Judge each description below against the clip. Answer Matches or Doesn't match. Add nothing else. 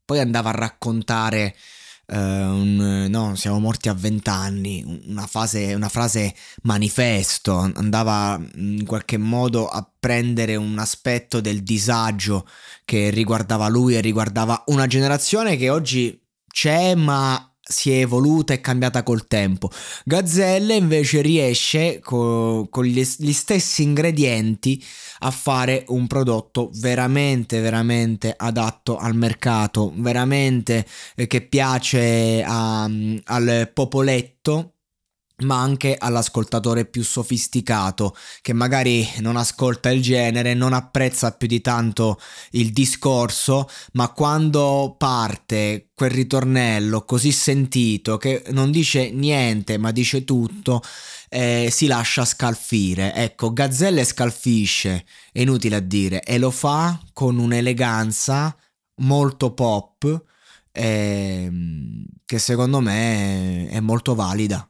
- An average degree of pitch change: Matches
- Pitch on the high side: Doesn't match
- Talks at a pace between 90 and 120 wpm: Matches